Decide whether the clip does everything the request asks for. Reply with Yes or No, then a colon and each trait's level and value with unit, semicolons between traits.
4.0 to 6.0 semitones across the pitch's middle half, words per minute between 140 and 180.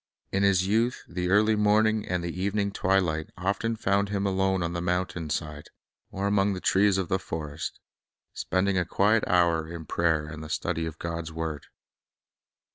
No: average, 3.2 semitones; average, 175 wpm